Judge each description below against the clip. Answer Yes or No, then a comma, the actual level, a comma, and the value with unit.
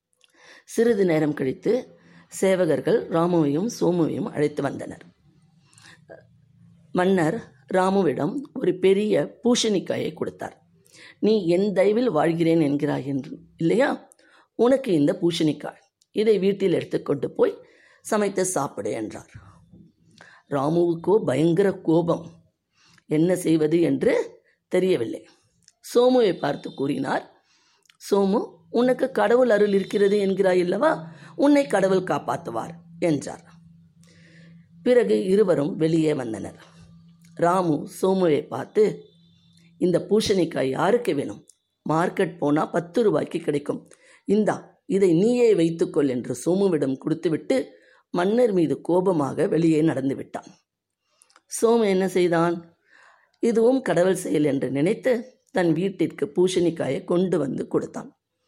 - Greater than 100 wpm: No, average, 95 wpm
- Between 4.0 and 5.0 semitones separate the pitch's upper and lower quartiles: Yes, average, 4.3 semitones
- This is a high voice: No, medium, 175 Hz